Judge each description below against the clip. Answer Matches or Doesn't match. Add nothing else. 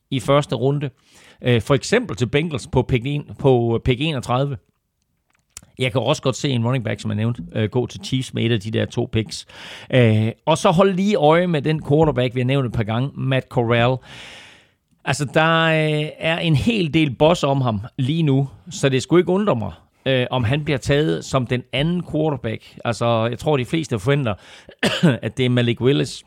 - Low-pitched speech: Matches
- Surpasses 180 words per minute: Matches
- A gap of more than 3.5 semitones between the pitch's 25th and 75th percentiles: Matches